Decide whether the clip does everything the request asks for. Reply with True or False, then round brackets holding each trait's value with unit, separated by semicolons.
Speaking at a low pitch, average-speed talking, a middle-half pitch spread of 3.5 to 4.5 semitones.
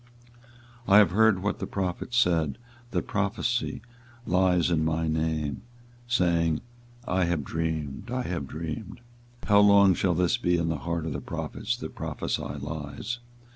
True (85 Hz; 160 wpm; 4.1 semitones)